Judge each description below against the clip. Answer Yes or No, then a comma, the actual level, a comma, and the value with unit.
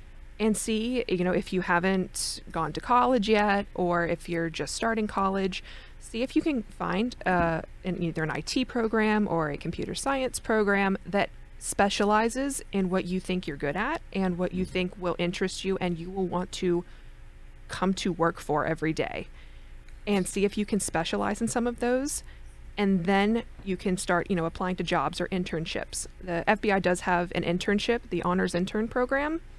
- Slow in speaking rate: No, average, 185 wpm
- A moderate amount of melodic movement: Yes, average, 3.5 semitones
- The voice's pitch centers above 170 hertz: Yes, high, 190 Hz